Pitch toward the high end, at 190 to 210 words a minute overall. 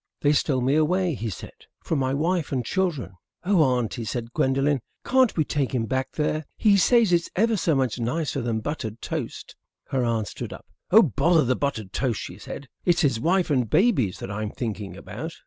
No: low, 135 Hz; average, 200 wpm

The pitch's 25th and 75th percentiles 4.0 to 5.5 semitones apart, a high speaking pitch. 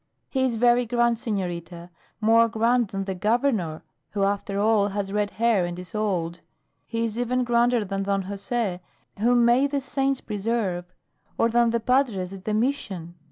No: average, 3.6 semitones; high, 220 Hz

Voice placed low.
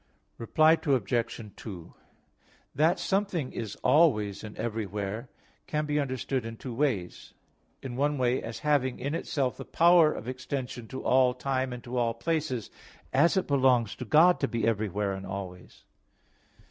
Yes: low, 125 Hz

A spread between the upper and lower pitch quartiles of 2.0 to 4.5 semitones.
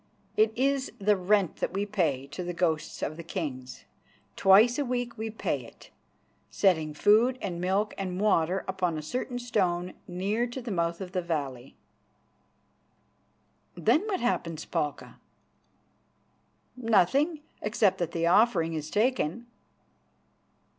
No: average, 5.3 semitones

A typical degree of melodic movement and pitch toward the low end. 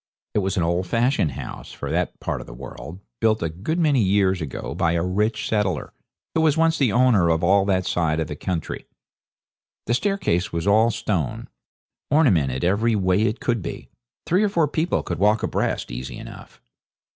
No: wide, 5.7 semitones; low, 100 Hz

